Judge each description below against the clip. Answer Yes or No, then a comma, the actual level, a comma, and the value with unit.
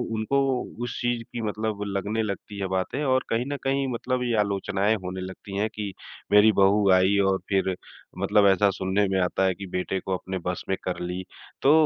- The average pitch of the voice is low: Yes, low, 100 Hz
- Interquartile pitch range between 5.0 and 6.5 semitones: No, average, 2.7 semitones